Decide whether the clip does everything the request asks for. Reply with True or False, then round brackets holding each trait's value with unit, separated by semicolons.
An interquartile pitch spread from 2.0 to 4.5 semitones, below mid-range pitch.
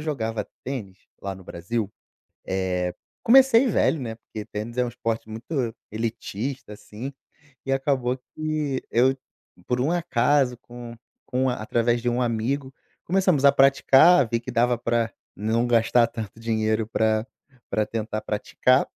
True (3.4 semitones; 120 Hz)